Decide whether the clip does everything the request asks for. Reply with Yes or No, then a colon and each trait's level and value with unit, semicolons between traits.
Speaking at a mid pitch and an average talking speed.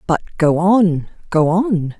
Yes: medium, 175 Hz; average, 150 wpm